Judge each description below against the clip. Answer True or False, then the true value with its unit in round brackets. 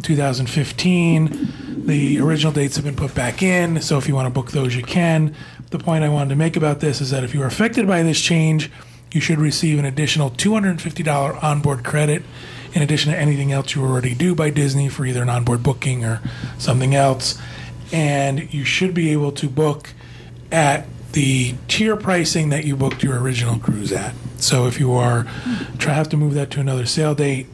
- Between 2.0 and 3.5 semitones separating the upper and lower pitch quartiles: True (3.0 semitones)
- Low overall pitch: False (145 Hz)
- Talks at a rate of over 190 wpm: True (200 wpm)